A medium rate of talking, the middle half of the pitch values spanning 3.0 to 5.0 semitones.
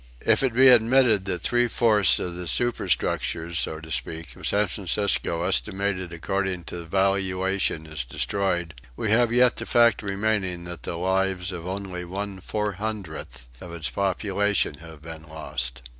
Yes: average, 160 wpm; average, 3.6 semitones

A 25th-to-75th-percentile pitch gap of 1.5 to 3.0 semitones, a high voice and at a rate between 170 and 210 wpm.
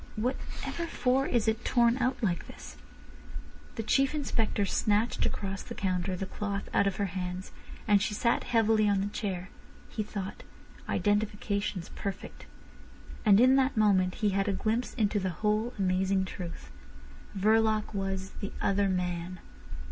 No: narrow, 2.6 semitones; high, 205 Hz; average, 150 wpm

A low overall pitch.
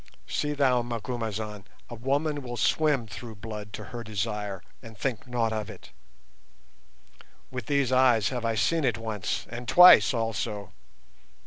Yes: low, 115 Hz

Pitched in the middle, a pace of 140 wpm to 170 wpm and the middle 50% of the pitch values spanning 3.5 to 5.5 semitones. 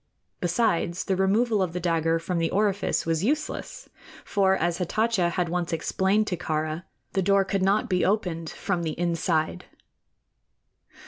No: medium, 180 Hz; average, 150 wpm; average, 3.0 semitones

